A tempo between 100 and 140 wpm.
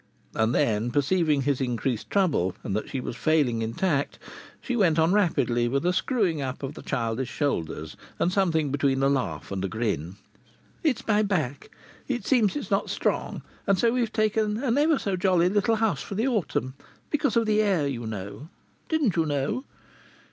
No: average, 185 wpm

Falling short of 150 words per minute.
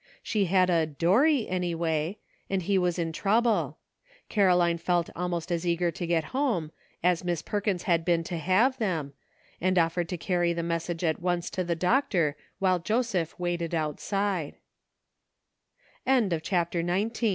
Yes: average, 140 wpm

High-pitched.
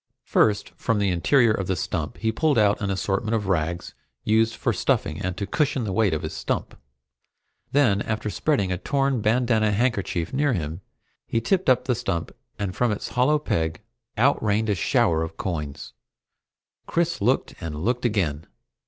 No: low, 105 Hz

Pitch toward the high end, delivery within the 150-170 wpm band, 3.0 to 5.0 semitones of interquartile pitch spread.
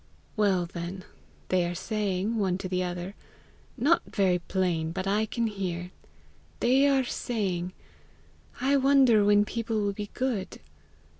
No: high, 200 Hz; average, 140 wpm; average, 4.0 semitones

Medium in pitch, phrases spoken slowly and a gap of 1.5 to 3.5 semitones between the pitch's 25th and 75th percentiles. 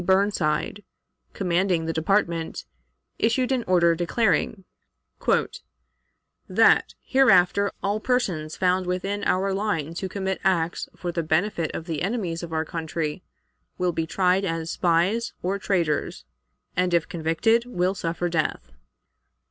Yes: medium, 180 Hz; slow, 125 wpm; average, 3.2 semitones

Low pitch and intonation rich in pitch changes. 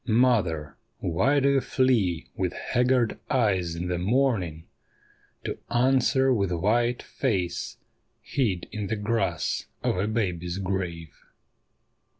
Yes: low, 105 Hz; wide, 5.9 semitones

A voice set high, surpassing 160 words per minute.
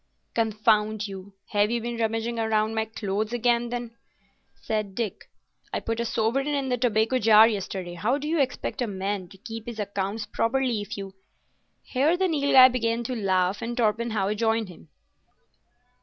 Yes: high, 225 Hz; average, 170 wpm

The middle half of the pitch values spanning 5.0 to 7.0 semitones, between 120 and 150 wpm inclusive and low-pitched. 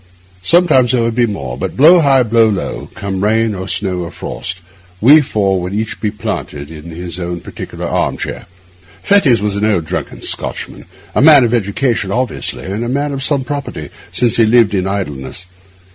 No: wide, 5.4 semitones; average, 190 wpm; low, 110 Hz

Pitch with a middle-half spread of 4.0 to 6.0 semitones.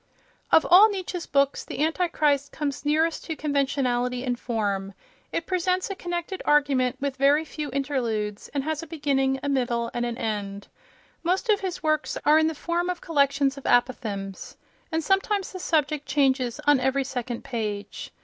Yes: average, 4.5 semitones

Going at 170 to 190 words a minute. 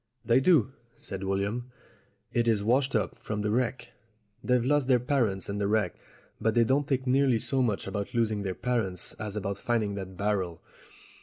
Yes: average, 180 wpm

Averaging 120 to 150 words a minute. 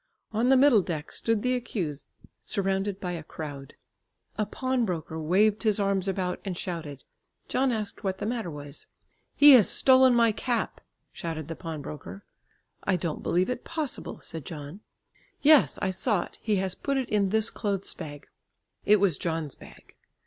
No: average, 165 wpm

